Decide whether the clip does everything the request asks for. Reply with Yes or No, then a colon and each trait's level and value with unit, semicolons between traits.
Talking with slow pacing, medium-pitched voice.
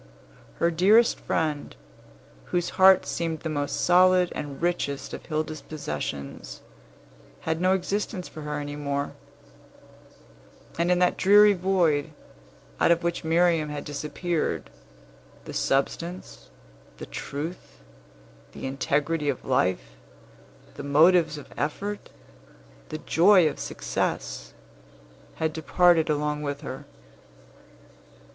Yes: slow, 110 wpm; medium, 160 Hz